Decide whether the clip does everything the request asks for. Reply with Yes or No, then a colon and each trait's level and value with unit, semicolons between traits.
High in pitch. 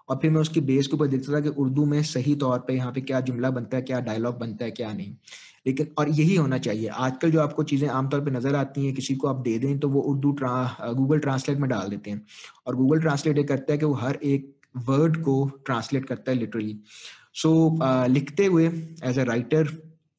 No: low, 135 Hz